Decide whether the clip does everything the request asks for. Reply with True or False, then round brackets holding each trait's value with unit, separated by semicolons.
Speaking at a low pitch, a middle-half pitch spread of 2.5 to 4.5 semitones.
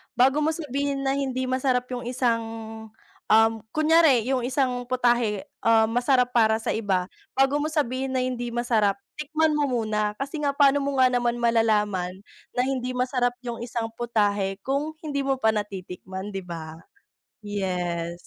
False (245 Hz; 4.1 semitones)